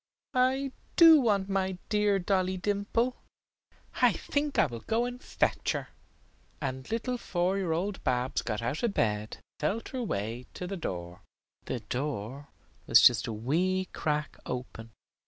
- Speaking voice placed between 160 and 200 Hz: Yes, medium, 185 Hz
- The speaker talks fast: No, average, 155 wpm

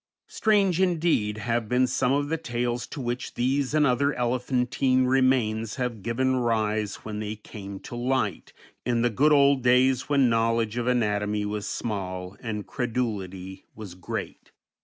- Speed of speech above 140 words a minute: Yes, average, 155 wpm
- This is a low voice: Yes, low, 120 Hz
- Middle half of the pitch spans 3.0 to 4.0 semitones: Yes, average, 3.5 semitones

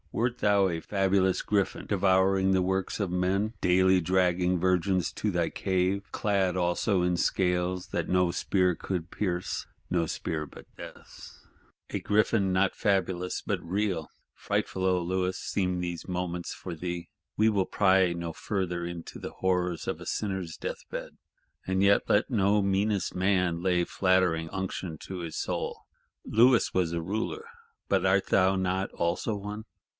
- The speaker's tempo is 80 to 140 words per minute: No, average, 150 wpm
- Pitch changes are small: Yes, narrow, 1.7 semitones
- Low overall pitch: Yes, very low, 95 Hz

